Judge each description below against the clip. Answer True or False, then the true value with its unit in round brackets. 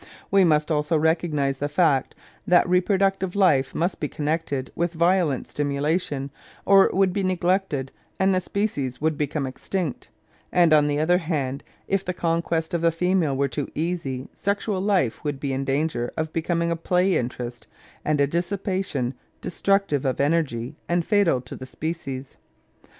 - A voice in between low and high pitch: True (160 Hz)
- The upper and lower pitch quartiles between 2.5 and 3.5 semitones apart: False (4.4 semitones)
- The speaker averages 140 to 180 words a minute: True (165 wpm)